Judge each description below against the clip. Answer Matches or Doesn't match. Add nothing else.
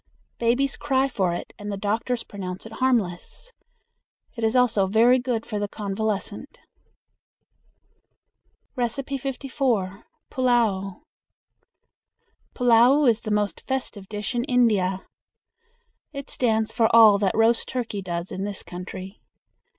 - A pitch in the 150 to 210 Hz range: Doesn't match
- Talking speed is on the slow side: Matches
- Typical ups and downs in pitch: Matches